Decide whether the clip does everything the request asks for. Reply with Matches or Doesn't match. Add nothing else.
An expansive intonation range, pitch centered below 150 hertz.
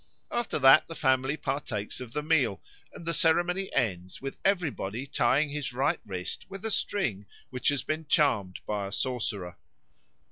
Matches